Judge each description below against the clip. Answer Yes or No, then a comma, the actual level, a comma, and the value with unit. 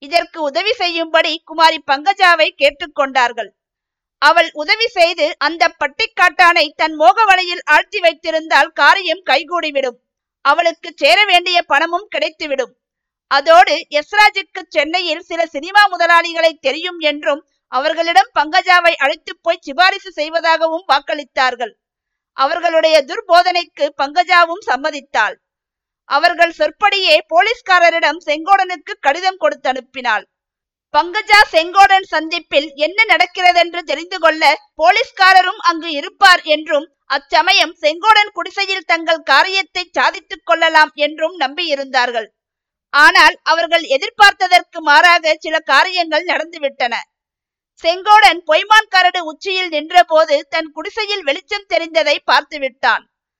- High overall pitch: Yes, very high, 330 Hz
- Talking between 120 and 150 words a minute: No, average, 100 wpm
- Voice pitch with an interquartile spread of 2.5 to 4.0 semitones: Yes, average, 3.3 semitones